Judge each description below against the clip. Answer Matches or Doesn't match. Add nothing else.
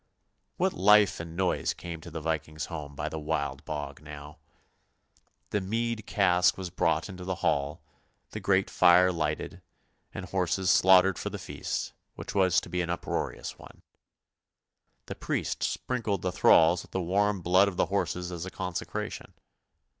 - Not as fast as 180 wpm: Matches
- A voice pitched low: Matches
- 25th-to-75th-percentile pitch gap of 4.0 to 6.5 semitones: Doesn't match